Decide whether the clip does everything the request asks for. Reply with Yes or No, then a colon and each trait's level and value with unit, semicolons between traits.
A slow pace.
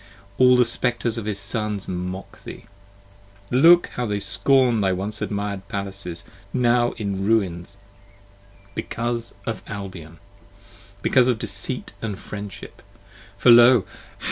Yes: slow, 120 wpm